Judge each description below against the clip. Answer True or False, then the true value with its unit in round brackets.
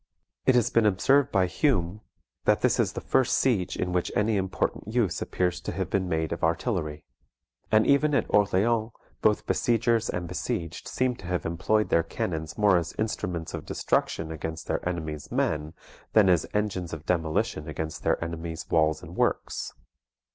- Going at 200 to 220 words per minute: False (170 wpm)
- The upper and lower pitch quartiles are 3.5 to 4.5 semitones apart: False (4.9 semitones)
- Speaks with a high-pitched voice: False (90 Hz)